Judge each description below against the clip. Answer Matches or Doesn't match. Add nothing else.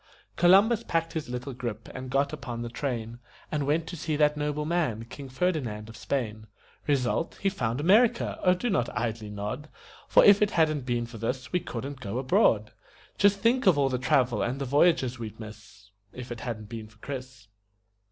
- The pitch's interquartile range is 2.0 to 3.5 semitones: Doesn't match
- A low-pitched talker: Matches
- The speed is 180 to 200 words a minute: Matches